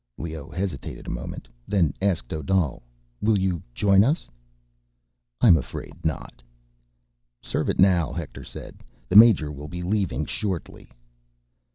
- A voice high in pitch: No, very low, 90 Hz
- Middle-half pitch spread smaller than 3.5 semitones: No, average, 4.1 semitones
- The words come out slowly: Yes, slow, 130 wpm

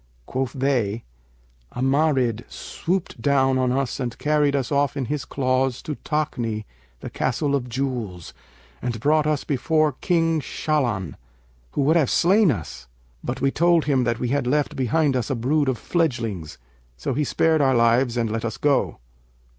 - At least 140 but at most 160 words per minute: No, average, 170 wpm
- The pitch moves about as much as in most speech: Yes, average, 3.8 semitones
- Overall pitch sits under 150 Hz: Yes, low, 135 Hz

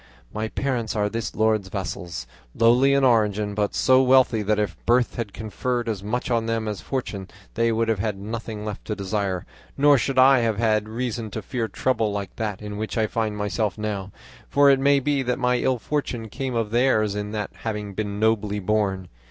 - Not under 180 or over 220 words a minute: Yes, average, 200 wpm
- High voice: No, low, 110 Hz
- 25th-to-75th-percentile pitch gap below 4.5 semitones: Yes, average, 2.9 semitones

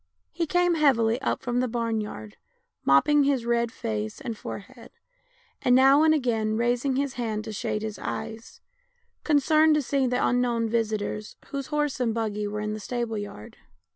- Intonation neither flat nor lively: Yes, average, 4.0 semitones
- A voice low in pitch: No, high, 235 Hz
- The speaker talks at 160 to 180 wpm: Yes, average, 170 wpm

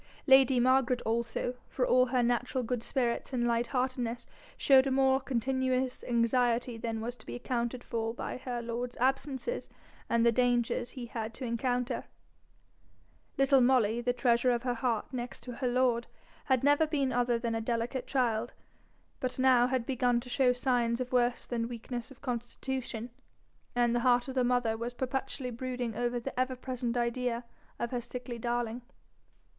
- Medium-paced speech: Yes, average, 170 wpm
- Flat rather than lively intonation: Yes, narrow, 1.5 semitones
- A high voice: Yes, high, 245 Hz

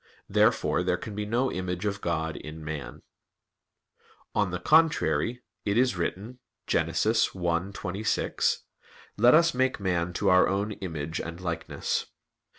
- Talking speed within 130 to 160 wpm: Yes, slow, 135 wpm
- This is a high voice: No, very low, 95 Hz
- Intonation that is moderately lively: Yes, average, 4.4 semitones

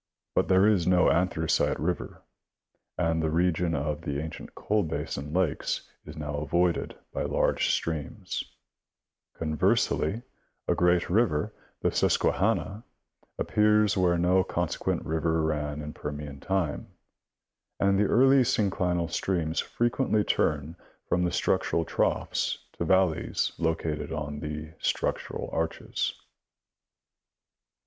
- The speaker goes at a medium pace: No, slow, 125 wpm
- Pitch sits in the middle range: No, very low, 85 Hz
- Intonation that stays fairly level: No, average, 3.4 semitones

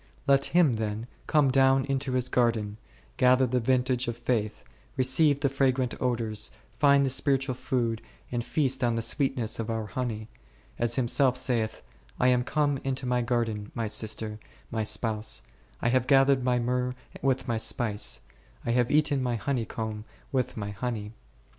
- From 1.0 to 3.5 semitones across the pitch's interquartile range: Yes, average, 2.8 semitones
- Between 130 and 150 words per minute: No, average, 165 wpm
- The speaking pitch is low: Yes, low, 125 Hz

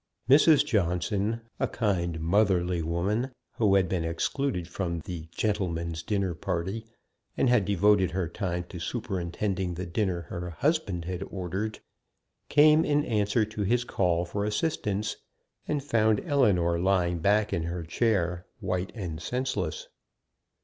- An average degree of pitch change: Yes, average, 4.0 semitones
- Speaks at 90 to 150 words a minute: Yes, slow, 135 wpm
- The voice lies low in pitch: Yes, very low, 95 Hz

